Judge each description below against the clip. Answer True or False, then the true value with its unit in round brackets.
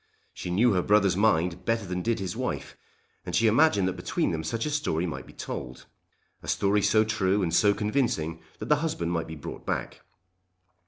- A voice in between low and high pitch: False (100 Hz)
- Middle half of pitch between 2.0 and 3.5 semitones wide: False (4.3 semitones)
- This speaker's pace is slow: False (200 wpm)